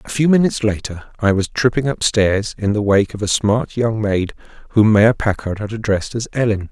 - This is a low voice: Yes, low, 110 Hz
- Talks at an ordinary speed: No, fast, 215 wpm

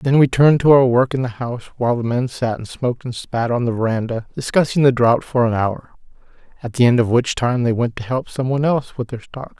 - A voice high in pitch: No, low, 125 Hz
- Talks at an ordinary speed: No, fast, 255 wpm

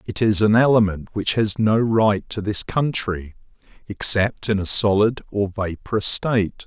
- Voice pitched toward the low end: Yes, low, 105 Hz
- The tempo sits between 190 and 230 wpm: No, average, 160 wpm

